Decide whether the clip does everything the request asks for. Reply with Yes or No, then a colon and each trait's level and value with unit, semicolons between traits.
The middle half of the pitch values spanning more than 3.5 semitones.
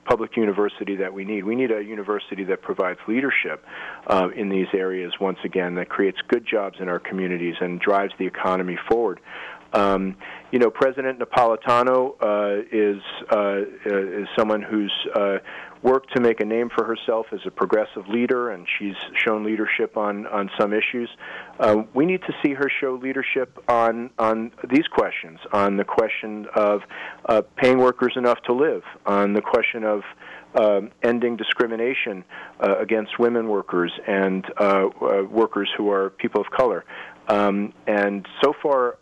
No: average, 3.0 semitones